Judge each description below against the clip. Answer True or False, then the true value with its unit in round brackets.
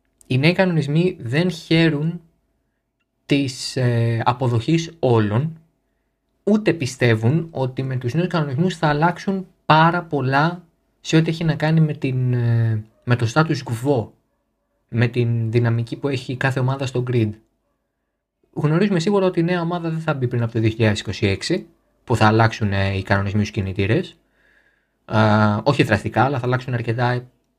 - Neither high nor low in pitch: False (130 Hz)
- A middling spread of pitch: False (5.7 semitones)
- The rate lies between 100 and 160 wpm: True (140 wpm)